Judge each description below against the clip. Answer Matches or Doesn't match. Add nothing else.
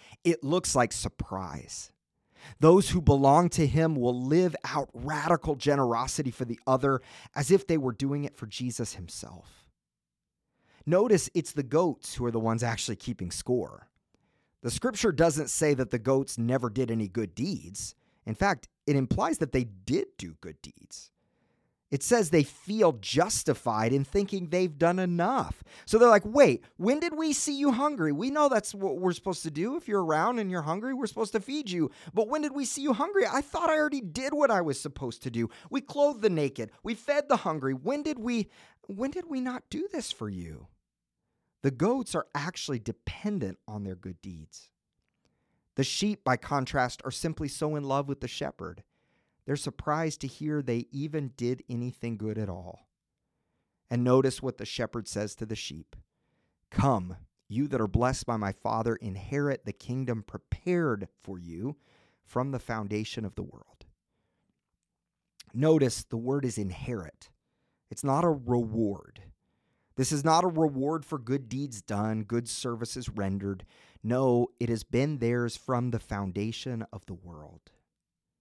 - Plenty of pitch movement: Matches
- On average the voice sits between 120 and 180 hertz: Matches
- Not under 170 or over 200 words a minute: Matches